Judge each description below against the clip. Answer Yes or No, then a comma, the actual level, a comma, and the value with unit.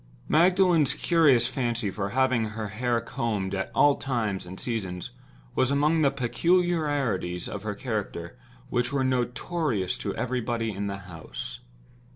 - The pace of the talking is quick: No, average, 140 wpm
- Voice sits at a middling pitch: No, low, 120 Hz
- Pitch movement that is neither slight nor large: No, wide, 5.7 semitones